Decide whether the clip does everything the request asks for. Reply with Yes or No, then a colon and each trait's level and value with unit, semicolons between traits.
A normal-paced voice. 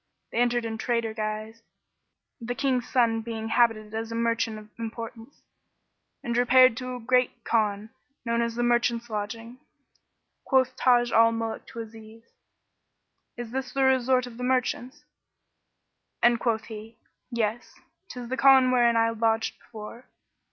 Yes: average, 145 wpm